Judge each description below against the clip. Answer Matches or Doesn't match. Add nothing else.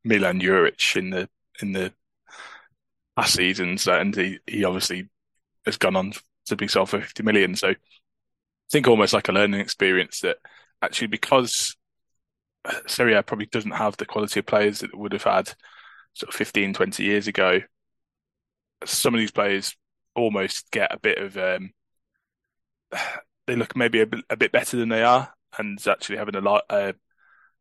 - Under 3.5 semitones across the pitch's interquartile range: Matches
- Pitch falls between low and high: Doesn't match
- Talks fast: Doesn't match